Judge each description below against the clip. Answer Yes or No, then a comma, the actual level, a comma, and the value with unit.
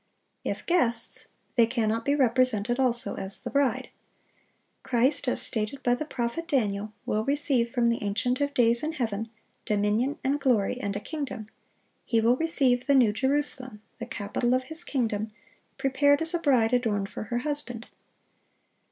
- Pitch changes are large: No, average, 3.8 semitones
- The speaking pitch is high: Yes, high, 245 Hz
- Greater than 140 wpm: Yes, average, 165 wpm